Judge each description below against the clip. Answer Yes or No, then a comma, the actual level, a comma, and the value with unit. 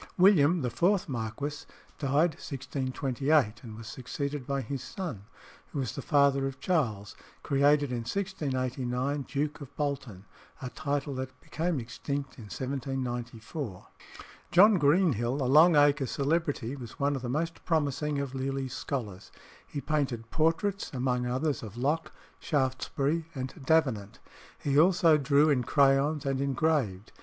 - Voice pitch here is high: No, medium, 140 Hz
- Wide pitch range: No, average, 3.1 semitones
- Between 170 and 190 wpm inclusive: No, average, 140 wpm